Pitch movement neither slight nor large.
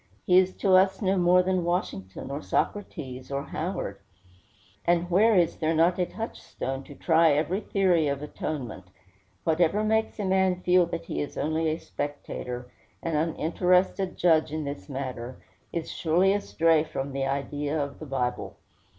Yes: average, 4.3 semitones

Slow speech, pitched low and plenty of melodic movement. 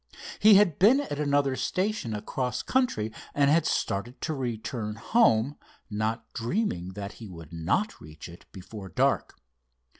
No: average, 145 wpm; low, 120 Hz; wide, 8.2 semitones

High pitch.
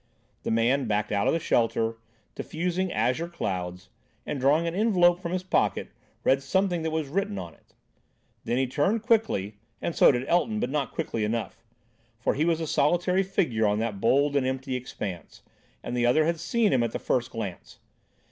No: medium, 140 Hz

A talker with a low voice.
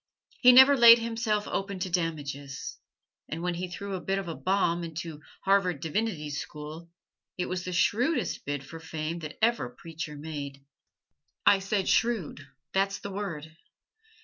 No: medium, 175 Hz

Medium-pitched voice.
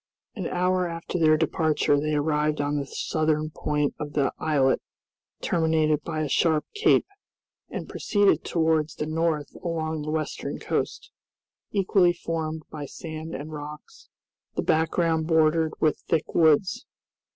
Yes: medium, 155 Hz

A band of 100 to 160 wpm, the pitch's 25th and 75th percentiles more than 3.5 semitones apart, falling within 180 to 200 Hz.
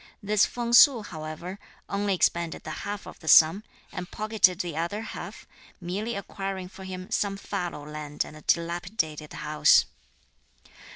Yes: average, 150 wpm; average, 4.1 semitones; medium, 185 Hz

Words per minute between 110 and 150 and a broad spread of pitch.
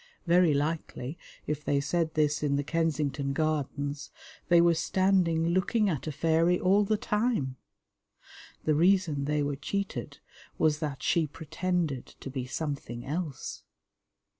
No: average, 140 wpm; average, 3.4 semitones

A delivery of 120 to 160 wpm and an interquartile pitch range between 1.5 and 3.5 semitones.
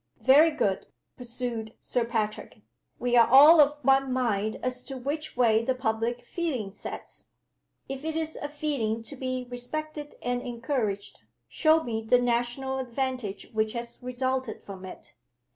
Yes: average, 150 wpm; average, 2.9 semitones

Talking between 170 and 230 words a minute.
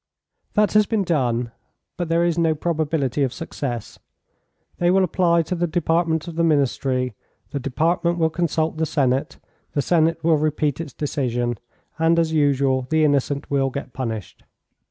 No: average, 160 wpm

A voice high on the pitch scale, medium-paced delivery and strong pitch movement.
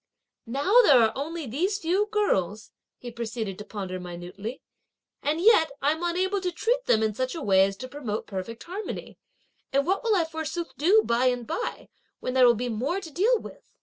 Yes: very high, 280 Hz; average, 195 wpm; wide, 8.5 semitones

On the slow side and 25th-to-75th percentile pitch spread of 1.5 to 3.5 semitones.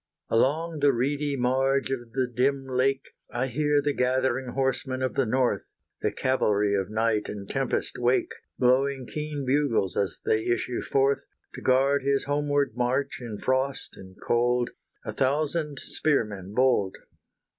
No: average, 145 wpm; narrow, 2.5 semitones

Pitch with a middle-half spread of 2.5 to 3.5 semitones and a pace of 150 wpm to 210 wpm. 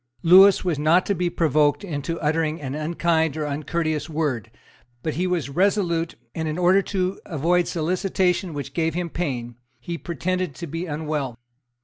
Yes: average, 2.8 semitones; average, 160 wpm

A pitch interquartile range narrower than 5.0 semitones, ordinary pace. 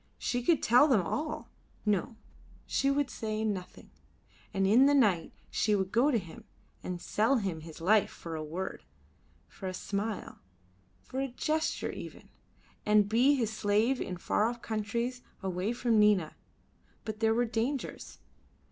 Yes: average, 4.2 semitones; average, 155 wpm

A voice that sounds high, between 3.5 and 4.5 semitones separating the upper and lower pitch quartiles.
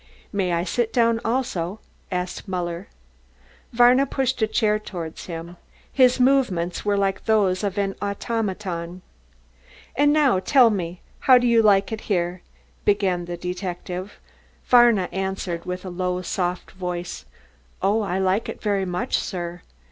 Yes: high, 195 Hz; average, 3.8 semitones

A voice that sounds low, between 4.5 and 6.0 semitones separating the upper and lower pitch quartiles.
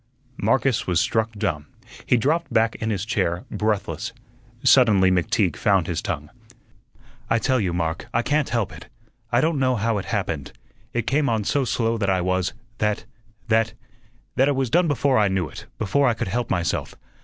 Yes: low, 110 Hz; average, 5.1 semitones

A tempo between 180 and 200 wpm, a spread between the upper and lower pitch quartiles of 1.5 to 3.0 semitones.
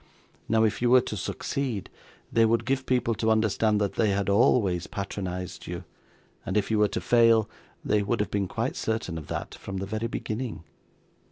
Yes: average, 190 wpm; narrow, 2.6 semitones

